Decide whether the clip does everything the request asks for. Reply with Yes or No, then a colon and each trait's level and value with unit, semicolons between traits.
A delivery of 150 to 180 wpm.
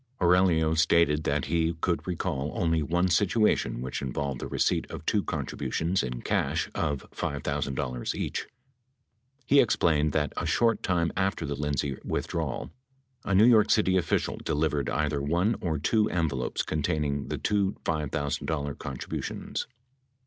No: average, 140 wpm